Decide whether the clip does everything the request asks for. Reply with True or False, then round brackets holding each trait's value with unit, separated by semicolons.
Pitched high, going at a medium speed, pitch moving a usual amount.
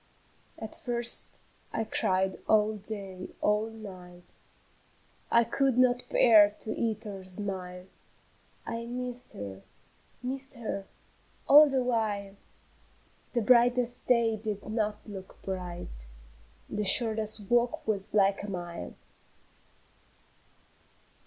False (215 Hz; 105 wpm; 3.5 semitones)